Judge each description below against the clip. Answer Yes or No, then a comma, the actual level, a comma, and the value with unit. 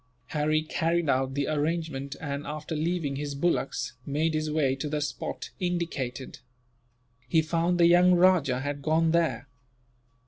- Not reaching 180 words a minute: Yes, average, 145 wpm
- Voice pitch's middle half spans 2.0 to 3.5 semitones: Yes, average, 3.0 semitones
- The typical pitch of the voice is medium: Yes, medium, 155 Hz